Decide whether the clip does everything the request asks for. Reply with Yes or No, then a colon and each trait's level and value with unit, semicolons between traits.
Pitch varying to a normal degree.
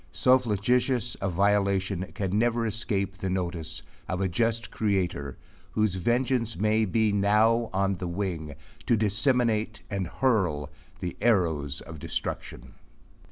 Yes: average, 3.9 semitones